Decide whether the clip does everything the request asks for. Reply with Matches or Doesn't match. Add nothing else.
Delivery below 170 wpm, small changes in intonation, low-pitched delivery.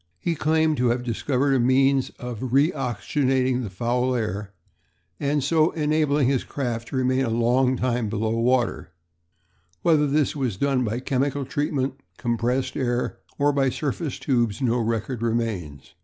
Doesn't match